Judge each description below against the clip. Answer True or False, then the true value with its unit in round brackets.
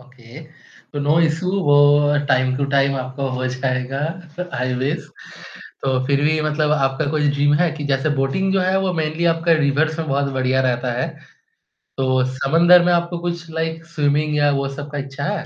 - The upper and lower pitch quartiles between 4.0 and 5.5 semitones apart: False (3.2 semitones)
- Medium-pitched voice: True (145 Hz)